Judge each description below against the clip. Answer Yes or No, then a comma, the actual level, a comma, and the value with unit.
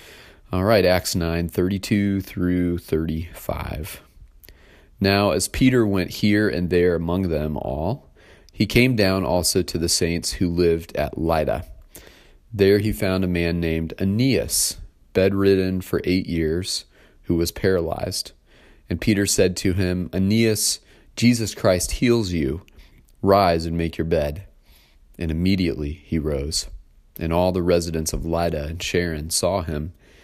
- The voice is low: Yes, very low, 90 Hz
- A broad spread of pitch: No, average, 3.1 semitones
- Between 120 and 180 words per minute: Yes, average, 140 wpm